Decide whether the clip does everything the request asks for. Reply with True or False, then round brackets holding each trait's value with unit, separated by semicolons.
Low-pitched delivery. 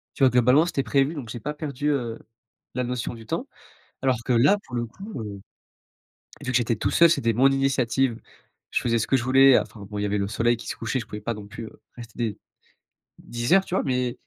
True (120 Hz)